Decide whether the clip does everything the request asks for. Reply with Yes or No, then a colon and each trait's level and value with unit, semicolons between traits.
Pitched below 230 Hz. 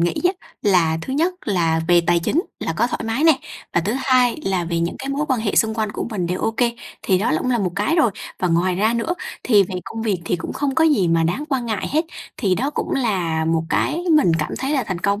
Yes: high, 210 Hz